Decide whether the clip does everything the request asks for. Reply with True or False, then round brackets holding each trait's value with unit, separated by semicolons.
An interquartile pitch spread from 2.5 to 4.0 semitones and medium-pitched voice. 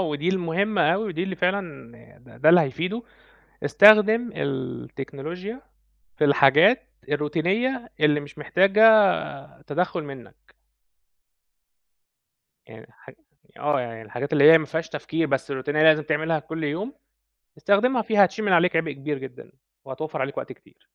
False (5.2 semitones; 160 Hz)